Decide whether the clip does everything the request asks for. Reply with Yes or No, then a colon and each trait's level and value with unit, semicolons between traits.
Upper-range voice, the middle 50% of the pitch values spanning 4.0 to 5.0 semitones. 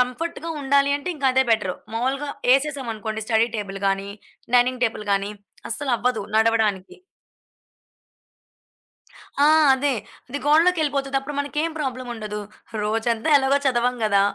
Yes: very high, 250 Hz; average, 4.3 semitones